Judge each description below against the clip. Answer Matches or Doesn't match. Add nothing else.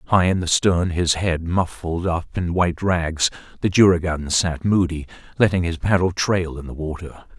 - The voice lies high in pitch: Doesn't match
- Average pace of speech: Matches